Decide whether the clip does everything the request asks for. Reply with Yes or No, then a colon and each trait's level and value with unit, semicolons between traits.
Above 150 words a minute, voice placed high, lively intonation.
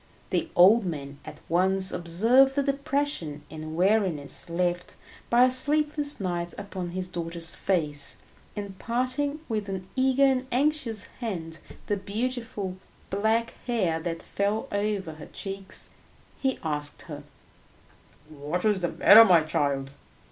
No: slow, 135 wpm; high, 195 Hz; wide, 6.1 semitones